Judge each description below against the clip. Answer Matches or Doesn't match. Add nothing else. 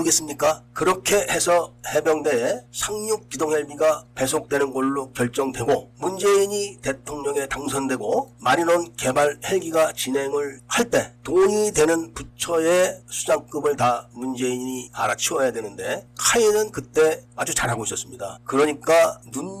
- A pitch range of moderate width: Matches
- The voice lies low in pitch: Doesn't match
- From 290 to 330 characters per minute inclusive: Matches